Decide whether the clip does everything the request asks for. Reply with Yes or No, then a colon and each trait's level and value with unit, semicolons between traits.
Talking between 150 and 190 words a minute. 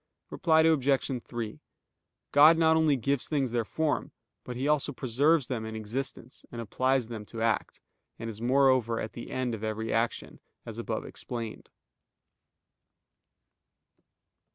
No: slow, 135 wpm